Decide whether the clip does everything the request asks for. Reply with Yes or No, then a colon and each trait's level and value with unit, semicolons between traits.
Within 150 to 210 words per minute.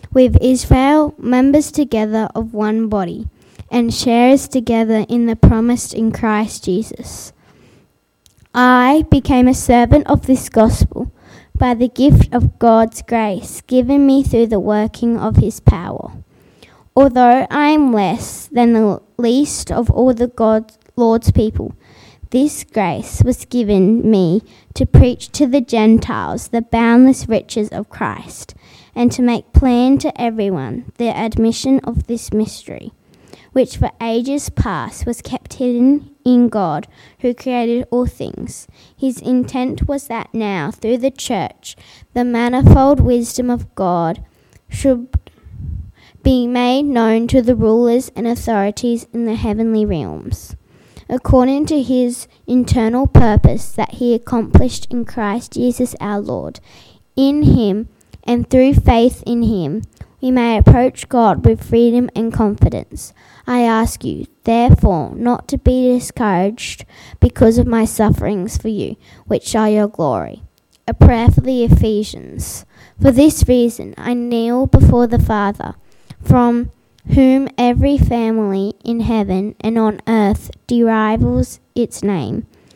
No: slow, 135 wpm